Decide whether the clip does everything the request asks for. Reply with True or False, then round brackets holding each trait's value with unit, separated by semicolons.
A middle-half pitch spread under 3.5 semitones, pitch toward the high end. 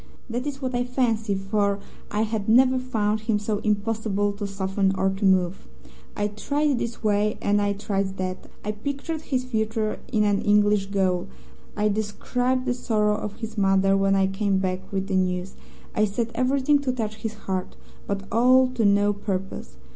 True (3.0 semitones; 210 Hz)